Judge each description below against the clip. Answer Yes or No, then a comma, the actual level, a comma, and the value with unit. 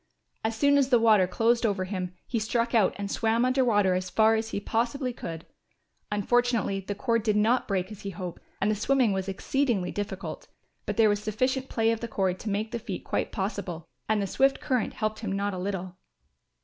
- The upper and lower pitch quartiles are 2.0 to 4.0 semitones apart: Yes, average, 3.2 semitones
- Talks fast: Yes, fast, 210 wpm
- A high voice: Yes, high, 215 Hz